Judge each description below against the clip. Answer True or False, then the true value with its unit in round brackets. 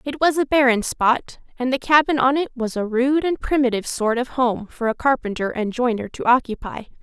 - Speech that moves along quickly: True (215 wpm)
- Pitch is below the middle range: False (250 Hz)